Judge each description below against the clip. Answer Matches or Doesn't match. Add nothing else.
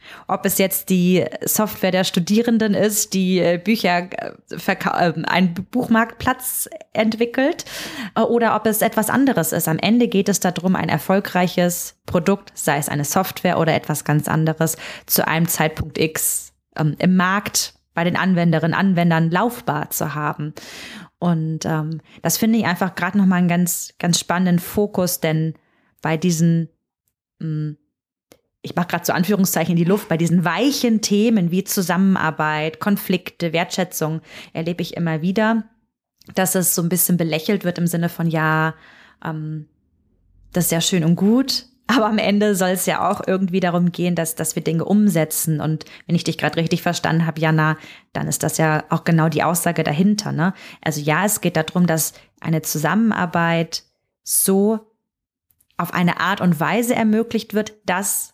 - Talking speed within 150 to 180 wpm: Matches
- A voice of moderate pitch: Matches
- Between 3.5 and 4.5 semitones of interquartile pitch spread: Matches